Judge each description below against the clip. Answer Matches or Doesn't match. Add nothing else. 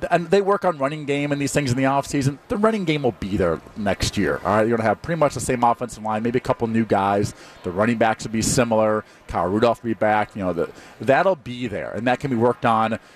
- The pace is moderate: Doesn't match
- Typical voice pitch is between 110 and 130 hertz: Matches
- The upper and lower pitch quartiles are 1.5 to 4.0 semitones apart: Doesn't match